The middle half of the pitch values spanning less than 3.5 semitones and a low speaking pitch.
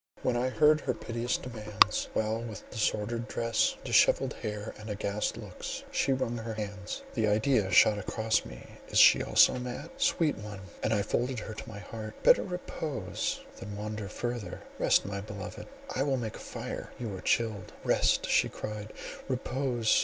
Yes: average, 2.9 semitones; low, 110 Hz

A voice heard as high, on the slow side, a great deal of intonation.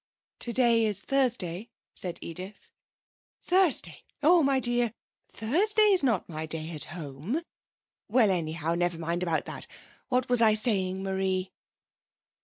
Yes: high, 205 Hz; slow, 125 wpm; wide, 6.5 semitones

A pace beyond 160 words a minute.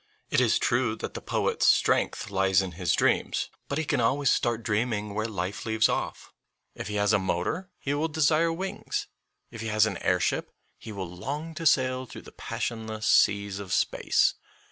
Yes: average, 190 wpm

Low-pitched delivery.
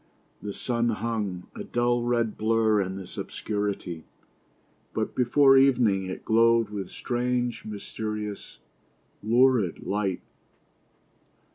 Yes: low, 110 Hz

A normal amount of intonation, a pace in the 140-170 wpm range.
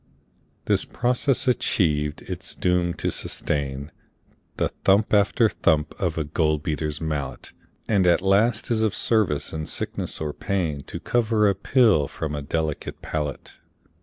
No: wide, 6.0 semitones; average, 150 wpm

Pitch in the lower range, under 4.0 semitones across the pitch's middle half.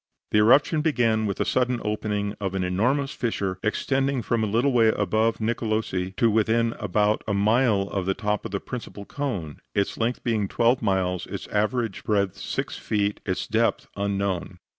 Yes: low, 110 Hz; average, 2.9 semitones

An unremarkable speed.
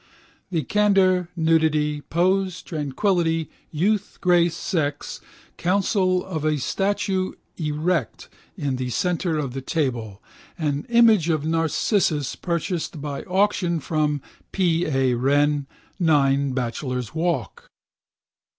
No: slow, 105 wpm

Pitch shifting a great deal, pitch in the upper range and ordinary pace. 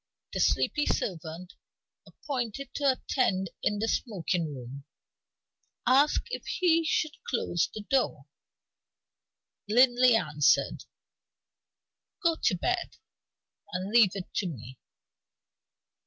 No: wide, 7.5 semitones; high, 215 Hz; slow, 100 wpm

